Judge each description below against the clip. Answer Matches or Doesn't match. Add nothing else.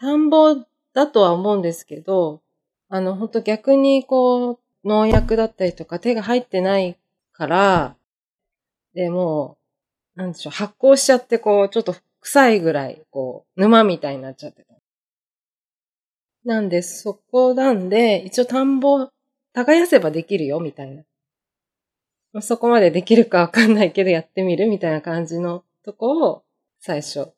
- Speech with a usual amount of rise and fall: Doesn't match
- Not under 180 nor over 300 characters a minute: Matches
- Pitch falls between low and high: Doesn't match